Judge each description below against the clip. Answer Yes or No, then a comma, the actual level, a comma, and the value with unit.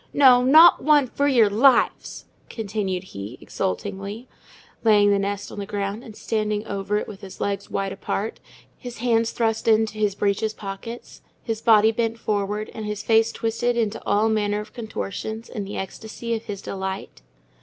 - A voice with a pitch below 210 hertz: No, high, 215 Hz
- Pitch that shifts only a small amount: Yes, narrow, 2.2 semitones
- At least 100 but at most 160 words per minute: No, average, 170 wpm